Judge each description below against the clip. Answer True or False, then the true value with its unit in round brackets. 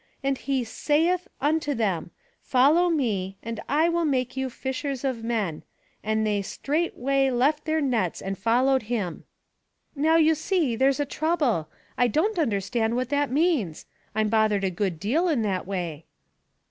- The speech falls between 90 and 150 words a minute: False (170 wpm)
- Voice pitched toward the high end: True (255 Hz)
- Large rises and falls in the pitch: True (5.7 semitones)